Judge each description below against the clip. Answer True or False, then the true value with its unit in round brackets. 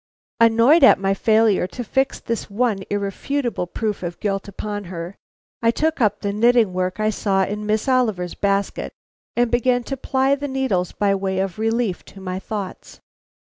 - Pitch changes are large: False (3.7 semitones)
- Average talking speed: True (170 wpm)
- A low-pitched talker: False (210 Hz)